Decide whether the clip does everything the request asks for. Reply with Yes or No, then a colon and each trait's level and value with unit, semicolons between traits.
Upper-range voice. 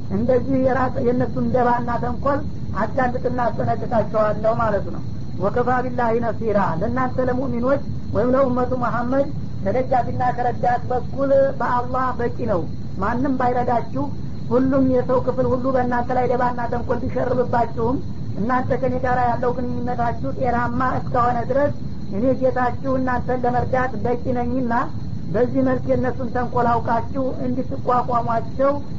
Yes: very high, 250 Hz